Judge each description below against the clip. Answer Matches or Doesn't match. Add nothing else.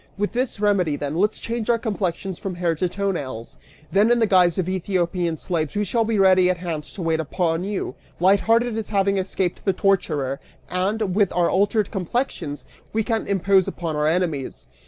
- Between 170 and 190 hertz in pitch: Matches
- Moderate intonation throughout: Matches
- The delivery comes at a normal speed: Matches